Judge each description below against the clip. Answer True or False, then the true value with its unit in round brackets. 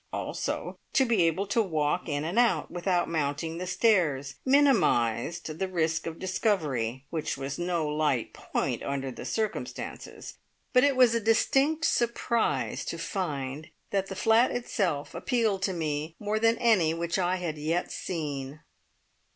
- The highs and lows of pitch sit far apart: True (6.4 semitones)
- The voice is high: False (175 Hz)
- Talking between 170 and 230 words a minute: False (150 wpm)